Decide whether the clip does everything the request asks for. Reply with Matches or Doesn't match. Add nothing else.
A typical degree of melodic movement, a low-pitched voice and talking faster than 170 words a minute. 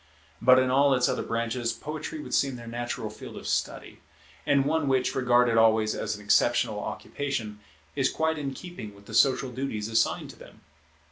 Matches